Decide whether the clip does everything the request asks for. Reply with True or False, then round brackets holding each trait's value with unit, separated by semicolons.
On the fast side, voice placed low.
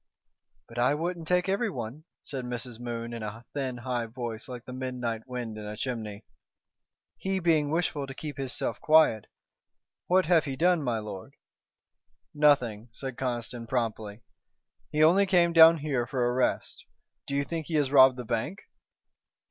False (165 wpm; 130 Hz)